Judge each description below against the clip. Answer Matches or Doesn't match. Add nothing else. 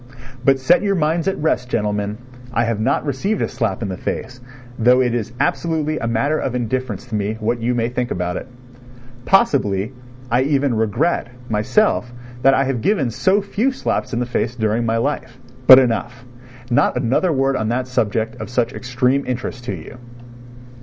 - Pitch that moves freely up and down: Doesn't match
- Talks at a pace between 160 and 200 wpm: Matches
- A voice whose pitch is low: Matches